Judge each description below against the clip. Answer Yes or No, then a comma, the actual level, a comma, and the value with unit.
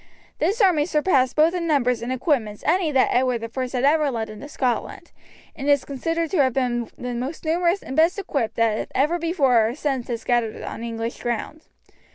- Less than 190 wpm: No, average, 195 wpm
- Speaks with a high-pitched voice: Yes, very high, 265 Hz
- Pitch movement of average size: Yes, average, 4.7 semitones